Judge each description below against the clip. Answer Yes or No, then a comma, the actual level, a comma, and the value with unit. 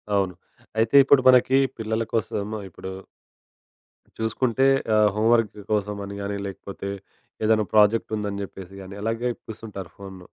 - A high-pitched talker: No, low, 105 Hz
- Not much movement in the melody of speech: Yes, narrow, 2.2 semitones